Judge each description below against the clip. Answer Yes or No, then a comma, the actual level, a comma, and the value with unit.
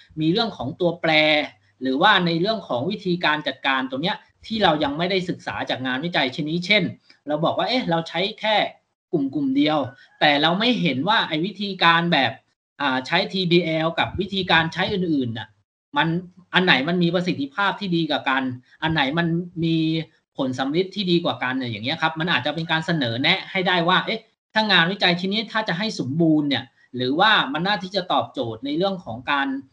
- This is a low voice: No, medium, 170 Hz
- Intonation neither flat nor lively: Yes, average, 4.1 semitones